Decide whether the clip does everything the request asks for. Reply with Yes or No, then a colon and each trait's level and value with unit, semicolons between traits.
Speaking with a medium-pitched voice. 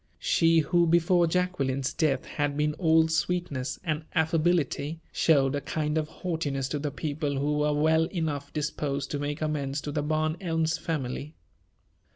Yes: medium, 155 Hz